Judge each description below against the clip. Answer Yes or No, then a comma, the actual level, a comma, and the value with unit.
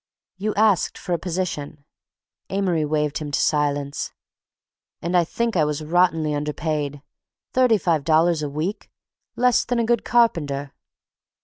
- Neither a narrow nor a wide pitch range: Yes, average, 4.5 semitones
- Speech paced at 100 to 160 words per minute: Yes, slow, 135 wpm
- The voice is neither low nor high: Yes, medium, 160 Hz